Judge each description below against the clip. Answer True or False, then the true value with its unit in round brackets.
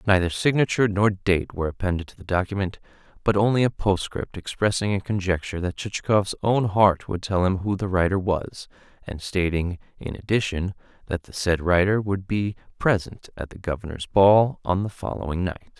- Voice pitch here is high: False (95 Hz)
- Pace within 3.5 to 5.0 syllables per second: False (5.4 syllables/s)